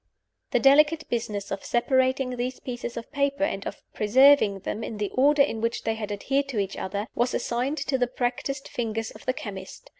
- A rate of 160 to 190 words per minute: No, average, 200 wpm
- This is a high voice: Yes, high, 245 Hz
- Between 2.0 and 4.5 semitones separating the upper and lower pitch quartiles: Yes, average, 4.1 semitones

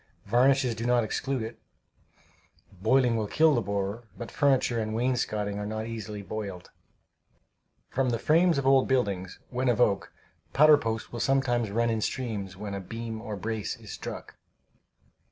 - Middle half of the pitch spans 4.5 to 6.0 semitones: No, average, 3.5 semitones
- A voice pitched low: Yes, low, 115 Hz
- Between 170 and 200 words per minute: No, average, 160 wpm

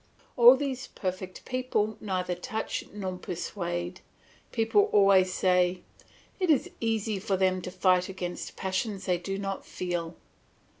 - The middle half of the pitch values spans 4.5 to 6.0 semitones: No, average, 3.1 semitones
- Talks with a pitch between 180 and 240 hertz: Yes, high, 190 Hz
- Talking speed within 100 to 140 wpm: Yes, slow, 135 wpm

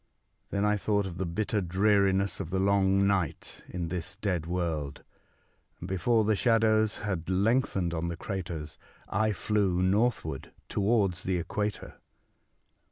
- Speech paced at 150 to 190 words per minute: No, average, 140 wpm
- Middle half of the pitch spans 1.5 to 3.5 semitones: Yes, average, 3.0 semitones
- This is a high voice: No, very low, 95 Hz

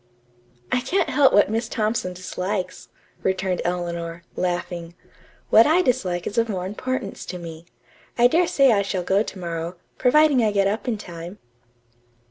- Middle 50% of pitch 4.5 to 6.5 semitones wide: Yes, average, 4.8 semitones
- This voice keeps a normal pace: Yes, average, 160 wpm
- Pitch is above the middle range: Yes, high, 195 Hz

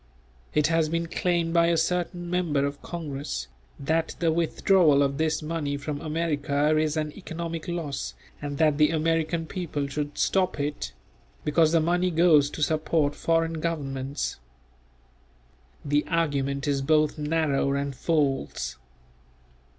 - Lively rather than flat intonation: No, narrow, 2.6 semitones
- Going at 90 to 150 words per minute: Yes, slow, 135 wpm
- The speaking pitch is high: No, medium, 155 Hz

